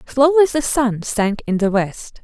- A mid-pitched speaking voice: No, high, 240 Hz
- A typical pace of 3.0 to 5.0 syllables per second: Yes, 4.4 syllables/s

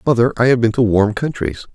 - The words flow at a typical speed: No, fast, 240 wpm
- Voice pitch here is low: Yes, low, 115 Hz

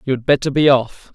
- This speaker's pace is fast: Yes, fast, 260 wpm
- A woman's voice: No, male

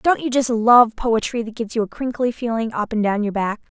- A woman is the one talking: Yes, female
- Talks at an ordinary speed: No, fast, 255 wpm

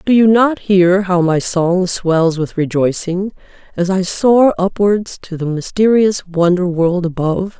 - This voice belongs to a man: No, female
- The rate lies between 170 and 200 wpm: No, average, 160 wpm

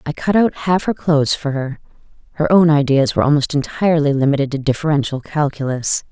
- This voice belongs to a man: No, female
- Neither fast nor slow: Yes, average, 175 wpm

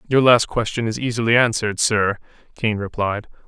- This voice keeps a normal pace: Yes, average, 155 wpm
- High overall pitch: No, low, 110 Hz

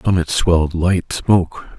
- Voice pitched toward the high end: No, very low, 85 Hz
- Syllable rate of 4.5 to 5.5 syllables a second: No, 4.3 syllables/s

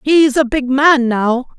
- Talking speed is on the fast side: No, average, 190 wpm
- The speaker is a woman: Yes, female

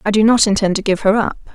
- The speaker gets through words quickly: Yes, fast, 310 wpm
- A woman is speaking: Yes, female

